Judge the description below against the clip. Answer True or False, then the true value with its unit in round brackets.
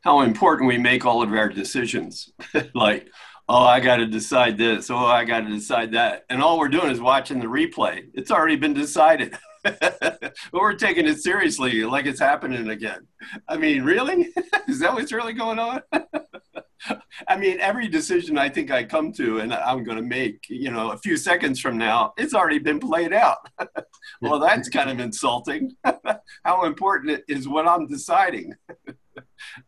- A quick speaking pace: False (175 wpm)